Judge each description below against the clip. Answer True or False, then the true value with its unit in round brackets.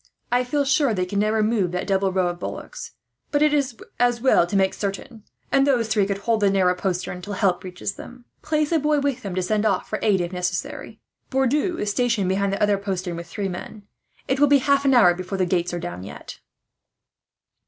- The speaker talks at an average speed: False (225 wpm)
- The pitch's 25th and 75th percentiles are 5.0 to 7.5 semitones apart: True (5.4 semitones)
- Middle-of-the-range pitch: False (205 Hz)